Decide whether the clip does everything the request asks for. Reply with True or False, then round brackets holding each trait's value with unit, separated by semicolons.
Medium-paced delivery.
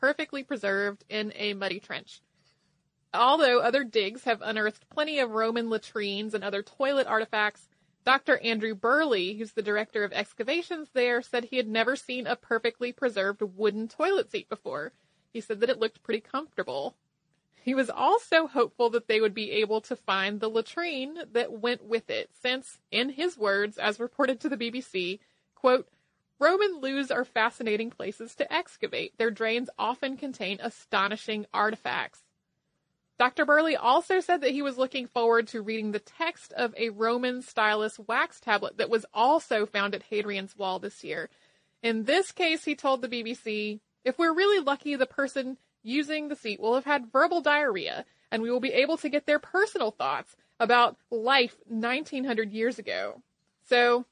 True (170 wpm)